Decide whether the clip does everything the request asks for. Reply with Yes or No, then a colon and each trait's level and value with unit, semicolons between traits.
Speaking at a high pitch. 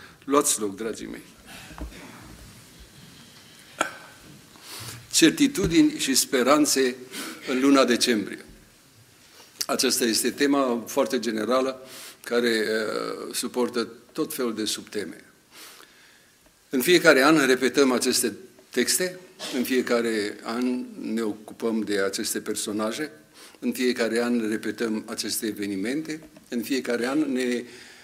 No: low, 125 Hz